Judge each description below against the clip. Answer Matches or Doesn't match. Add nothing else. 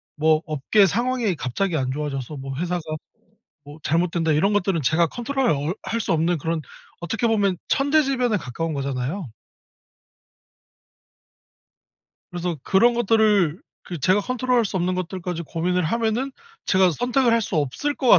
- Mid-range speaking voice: Matches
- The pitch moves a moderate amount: Doesn't match